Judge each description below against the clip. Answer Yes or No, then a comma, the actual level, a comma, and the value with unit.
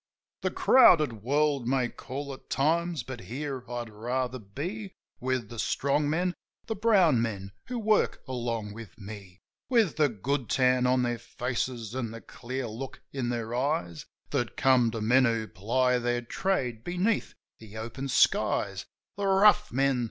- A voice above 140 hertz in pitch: No, low, 130 Hz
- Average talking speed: Yes, average, 160 wpm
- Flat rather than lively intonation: No, average, 4.3 semitones